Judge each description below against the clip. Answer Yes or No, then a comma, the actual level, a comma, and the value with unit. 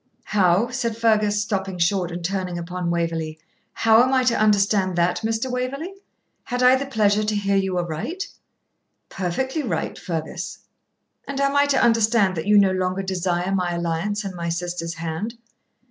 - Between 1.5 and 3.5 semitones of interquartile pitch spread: No, average, 4.6 semitones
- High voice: Yes, high, 195 Hz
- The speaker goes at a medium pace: Yes, average, 165 wpm